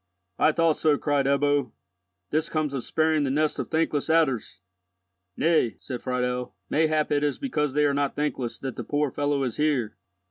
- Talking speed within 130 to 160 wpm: No, average, 180 wpm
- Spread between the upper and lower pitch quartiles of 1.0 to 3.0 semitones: Yes, narrow, 2.5 semitones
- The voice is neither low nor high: Yes, medium, 145 Hz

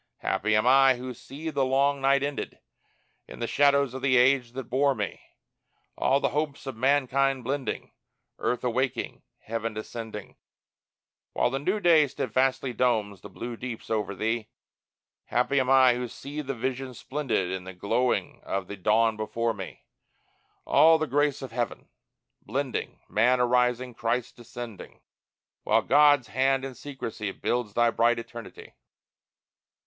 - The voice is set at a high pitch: No, low, 125 Hz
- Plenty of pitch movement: No, average, 3.0 semitones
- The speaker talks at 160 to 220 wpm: No, average, 150 wpm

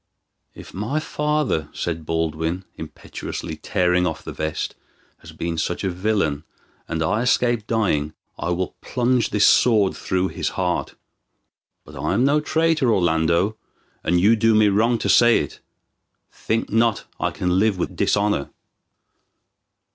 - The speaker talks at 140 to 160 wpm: Yes, average, 145 wpm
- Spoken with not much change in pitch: No, wide, 5.5 semitones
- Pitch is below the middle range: Yes, low, 100 Hz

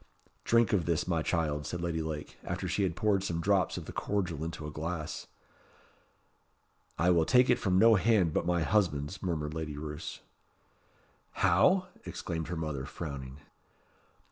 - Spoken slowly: No, average, 160 wpm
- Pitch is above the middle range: No, very low, 85 Hz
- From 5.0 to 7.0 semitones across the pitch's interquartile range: No, average, 3.7 semitones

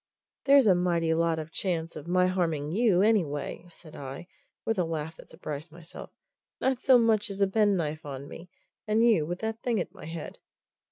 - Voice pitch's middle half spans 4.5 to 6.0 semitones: Yes, average, 4.8 semitones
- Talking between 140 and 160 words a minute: No, average, 190 wpm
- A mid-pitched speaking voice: Yes, medium, 175 Hz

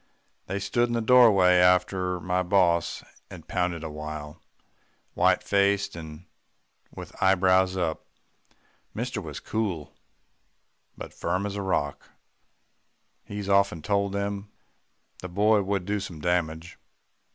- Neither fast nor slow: No, slow, 125 wpm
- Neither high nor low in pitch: No, very low, 95 Hz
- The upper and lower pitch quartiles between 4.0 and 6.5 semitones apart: No, average, 2.7 semitones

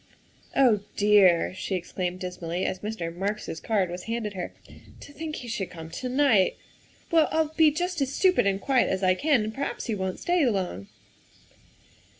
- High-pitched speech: Yes, high, 210 Hz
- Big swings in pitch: Yes, wide, 6.9 semitones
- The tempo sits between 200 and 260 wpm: Yes, fast, 205 wpm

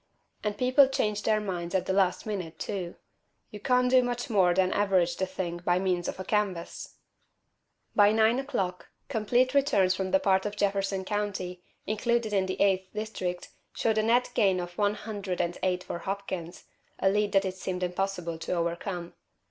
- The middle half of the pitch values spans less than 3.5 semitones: Yes, average, 2.8 semitones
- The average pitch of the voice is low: No, high, 195 Hz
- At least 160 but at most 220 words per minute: Yes, average, 180 wpm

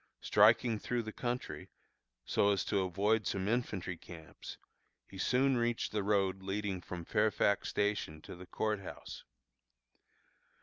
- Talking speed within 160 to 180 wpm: No, slow, 135 wpm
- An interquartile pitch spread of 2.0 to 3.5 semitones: Yes, average, 2.8 semitones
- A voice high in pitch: No, low, 105 Hz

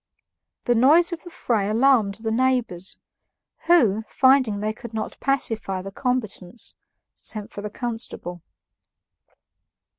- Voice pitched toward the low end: No, high, 225 Hz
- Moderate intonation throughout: Yes, average, 4.0 semitones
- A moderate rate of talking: No, slow, 120 wpm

